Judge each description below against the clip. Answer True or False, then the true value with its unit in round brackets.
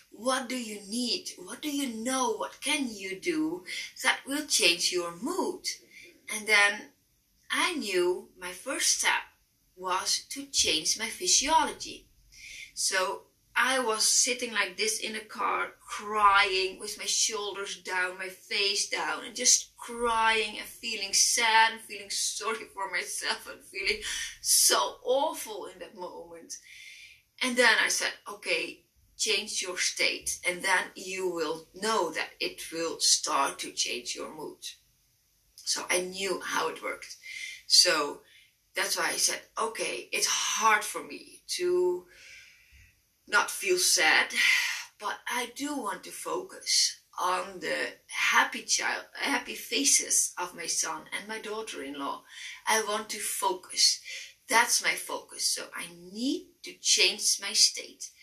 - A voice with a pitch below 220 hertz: False (245 Hz)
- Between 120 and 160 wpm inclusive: True (140 wpm)